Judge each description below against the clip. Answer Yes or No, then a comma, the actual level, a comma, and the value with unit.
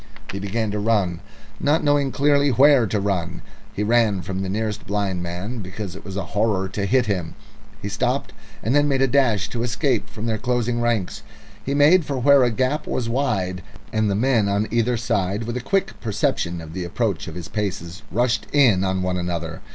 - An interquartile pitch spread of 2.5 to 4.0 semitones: No, average, 4.7 semitones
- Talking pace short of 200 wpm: No, fast, 205 wpm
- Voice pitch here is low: Yes, low, 110 Hz